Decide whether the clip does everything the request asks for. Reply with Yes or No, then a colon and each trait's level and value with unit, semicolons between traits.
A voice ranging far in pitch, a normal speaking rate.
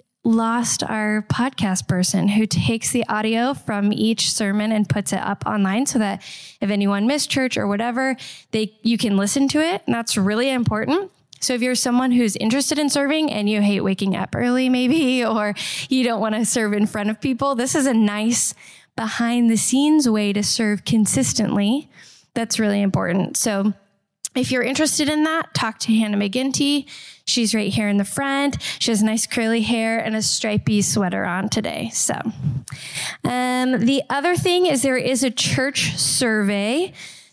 No: average, 3.8 semitones; average, 180 wpm